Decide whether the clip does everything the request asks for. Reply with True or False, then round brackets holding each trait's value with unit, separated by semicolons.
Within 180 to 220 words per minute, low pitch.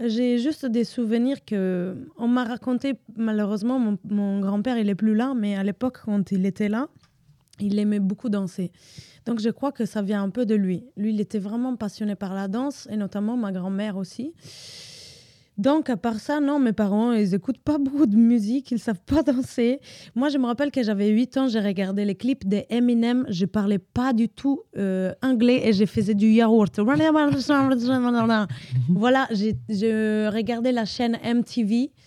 False (190 wpm; 225 Hz)